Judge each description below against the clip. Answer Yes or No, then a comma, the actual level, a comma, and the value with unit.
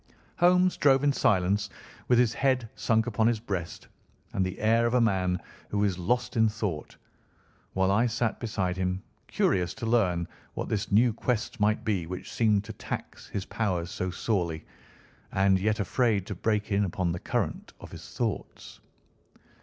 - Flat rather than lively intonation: No, average, 3.8 semitones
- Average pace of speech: Yes, average, 170 wpm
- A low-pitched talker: Yes, low, 105 Hz